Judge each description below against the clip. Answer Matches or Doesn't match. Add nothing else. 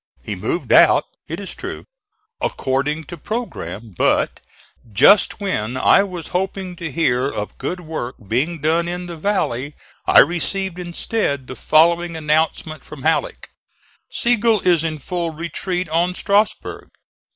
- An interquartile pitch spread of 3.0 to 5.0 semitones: Matches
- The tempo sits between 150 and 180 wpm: Doesn't match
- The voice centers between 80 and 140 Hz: Doesn't match